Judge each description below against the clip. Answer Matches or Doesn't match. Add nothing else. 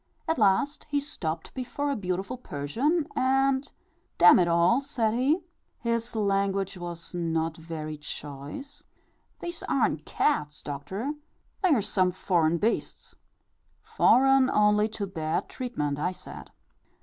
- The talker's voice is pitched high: Matches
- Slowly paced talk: Matches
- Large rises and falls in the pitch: Matches